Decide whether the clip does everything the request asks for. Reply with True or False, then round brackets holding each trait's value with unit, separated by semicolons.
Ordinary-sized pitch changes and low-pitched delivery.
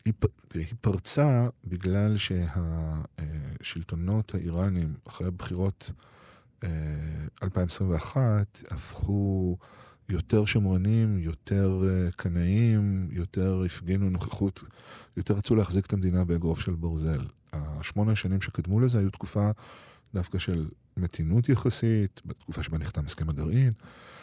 True (3.7 semitones; 95 Hz)